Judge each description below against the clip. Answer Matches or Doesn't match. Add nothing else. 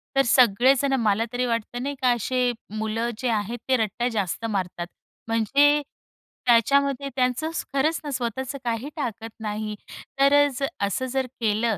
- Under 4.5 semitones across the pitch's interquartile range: Matches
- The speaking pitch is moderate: Doesn't match